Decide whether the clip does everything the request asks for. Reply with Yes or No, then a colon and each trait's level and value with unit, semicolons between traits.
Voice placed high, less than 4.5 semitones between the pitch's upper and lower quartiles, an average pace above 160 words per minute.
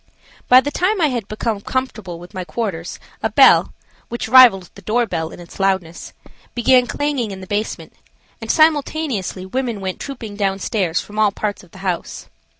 No: high, 215 Hz; average, 5.0 semitones; average, 180 wpm